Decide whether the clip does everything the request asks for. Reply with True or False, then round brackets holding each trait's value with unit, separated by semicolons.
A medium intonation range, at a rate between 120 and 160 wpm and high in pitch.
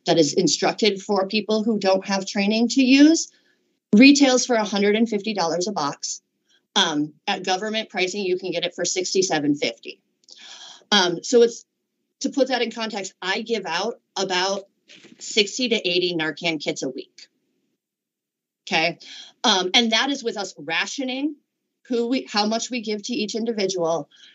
True (4.3 semitones; 155 wpm; 210 Hz)